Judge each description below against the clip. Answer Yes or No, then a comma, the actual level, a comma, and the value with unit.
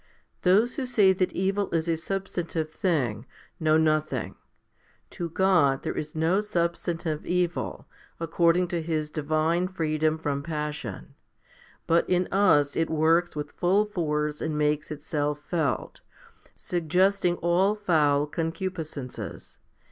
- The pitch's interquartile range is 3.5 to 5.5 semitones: No, average, 3.1 semitones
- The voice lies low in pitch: No, medium, 165 Hz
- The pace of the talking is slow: Yes, slow, 125 wpm